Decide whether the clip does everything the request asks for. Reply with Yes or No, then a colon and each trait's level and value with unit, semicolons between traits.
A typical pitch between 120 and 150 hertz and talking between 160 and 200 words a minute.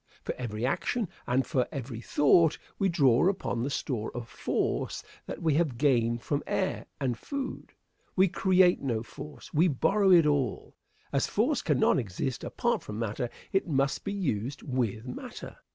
Yes: medium, 140 Hz; average, 165 wpm